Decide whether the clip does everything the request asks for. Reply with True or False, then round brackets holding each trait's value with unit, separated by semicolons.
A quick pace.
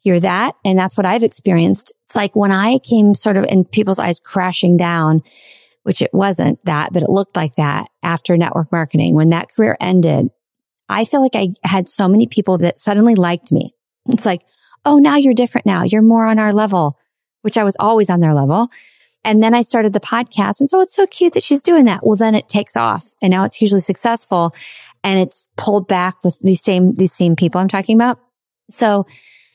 True (215 wpm)